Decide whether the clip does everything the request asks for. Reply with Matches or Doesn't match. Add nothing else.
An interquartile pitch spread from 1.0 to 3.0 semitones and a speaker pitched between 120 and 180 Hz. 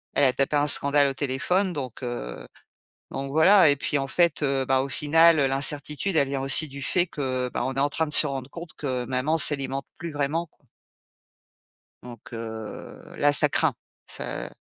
Matches